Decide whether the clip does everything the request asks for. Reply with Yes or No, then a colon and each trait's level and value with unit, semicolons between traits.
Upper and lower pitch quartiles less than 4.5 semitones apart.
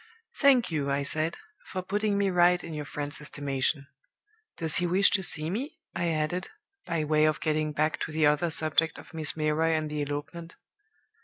Yes: narrow, 2.5 semitones